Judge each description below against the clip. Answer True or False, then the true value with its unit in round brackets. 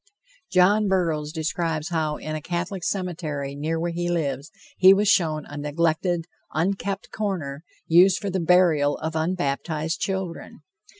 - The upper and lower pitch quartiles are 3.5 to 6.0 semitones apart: False (3.1 semitones)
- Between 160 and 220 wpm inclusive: False (140 wpm)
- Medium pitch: True (165 Hz)